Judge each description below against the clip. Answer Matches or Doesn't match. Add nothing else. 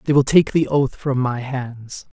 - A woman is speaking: Doesn't match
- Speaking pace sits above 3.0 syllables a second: Matches